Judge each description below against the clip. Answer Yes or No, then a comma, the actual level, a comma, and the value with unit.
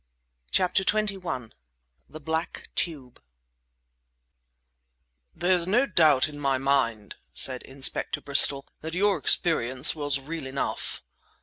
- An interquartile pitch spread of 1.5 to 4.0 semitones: No, average, 4.7 semitones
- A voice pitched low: No, medium, 150 Hz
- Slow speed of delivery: Yes, slow, 105 wpm